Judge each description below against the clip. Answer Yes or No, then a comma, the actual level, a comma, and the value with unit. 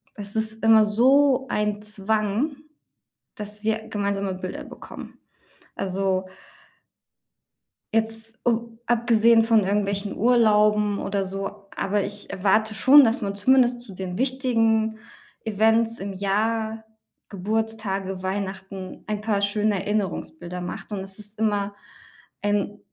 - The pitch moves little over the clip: Yes, narrow, 2.1 semitones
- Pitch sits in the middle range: No, high, 210 Hz